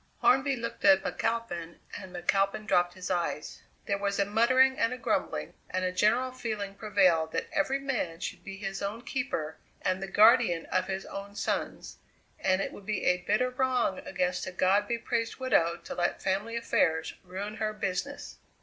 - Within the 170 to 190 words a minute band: Yes, average, 180 wpm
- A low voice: No, high, 200 Hz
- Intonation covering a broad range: No, average, 4.1 semitones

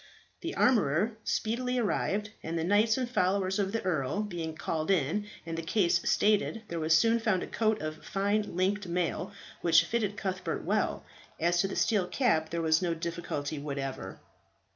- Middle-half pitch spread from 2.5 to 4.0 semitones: No, average, 4.5 semitones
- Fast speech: No, average, 175 wpm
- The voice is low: No, medium, 185 Hz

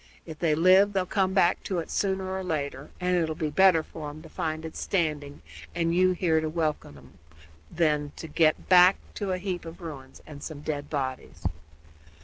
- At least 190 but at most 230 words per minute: Yes, average, 200 wpm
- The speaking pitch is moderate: Yes, medium, 160 Hz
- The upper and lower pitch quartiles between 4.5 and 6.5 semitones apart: No, average, 3.4 semitones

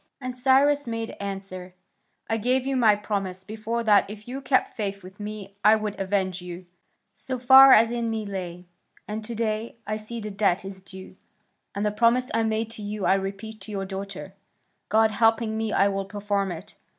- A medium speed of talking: Yes, average, 195 wpm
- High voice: Yes, high, 215 Hz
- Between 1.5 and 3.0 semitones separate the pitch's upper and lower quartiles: Yes, narrow, 2.6 semitones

